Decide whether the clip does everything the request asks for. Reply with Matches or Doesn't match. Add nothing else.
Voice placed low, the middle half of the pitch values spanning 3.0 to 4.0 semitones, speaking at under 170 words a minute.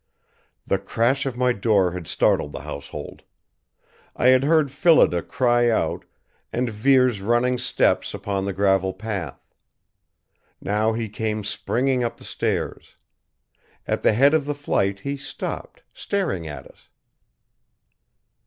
Doesn't match